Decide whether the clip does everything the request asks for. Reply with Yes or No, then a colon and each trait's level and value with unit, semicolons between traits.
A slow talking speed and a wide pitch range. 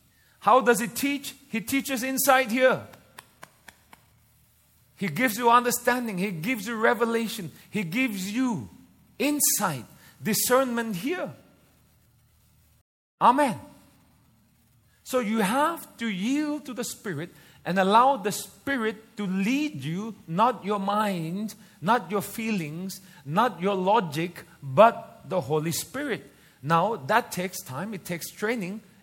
No: slow, 120 wpm; average, 4.9 semitones